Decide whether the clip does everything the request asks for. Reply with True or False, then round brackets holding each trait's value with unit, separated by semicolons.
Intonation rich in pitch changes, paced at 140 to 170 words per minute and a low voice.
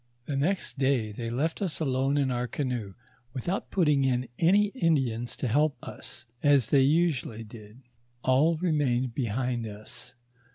False (4.0 semitones; 160 wpm; 130 Hz)